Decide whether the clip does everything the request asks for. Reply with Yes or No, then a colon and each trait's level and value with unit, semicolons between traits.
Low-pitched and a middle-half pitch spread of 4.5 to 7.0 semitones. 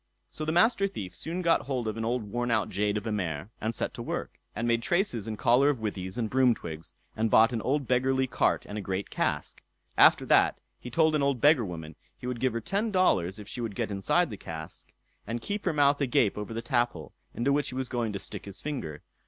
Yes: low, 120 Hz; average, 5.1 semitones